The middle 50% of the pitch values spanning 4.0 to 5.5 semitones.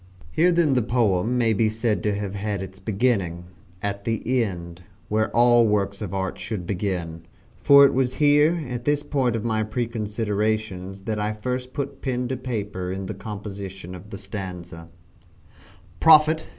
Yes: average, 4.3 semitones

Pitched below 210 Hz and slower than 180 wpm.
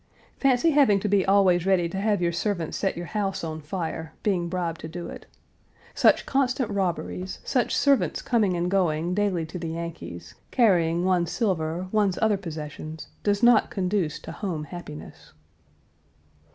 Yes: medium, 185 Hz; average, 160 wpm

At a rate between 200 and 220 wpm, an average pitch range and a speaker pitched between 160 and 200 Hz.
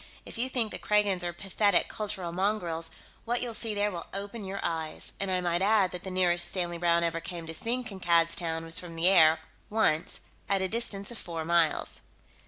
Yes: fast, 205 wpm; average, 3.5 semitones; medium, 185 Hz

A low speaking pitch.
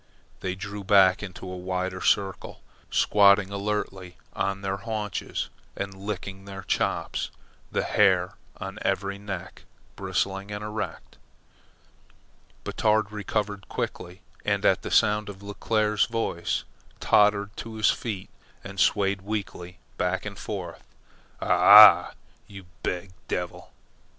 Yes: low, 100 Hz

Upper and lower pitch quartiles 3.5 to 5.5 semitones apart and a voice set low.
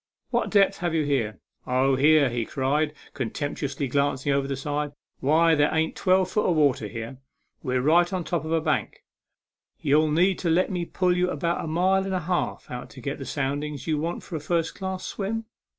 No: average, 4.0 semitones; medium, 155 Hz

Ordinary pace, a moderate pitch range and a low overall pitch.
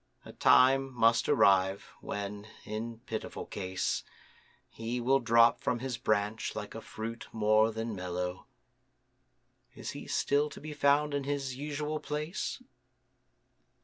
No: slow, 130 wpm; average, 4.7 semitones; low, 115 Hz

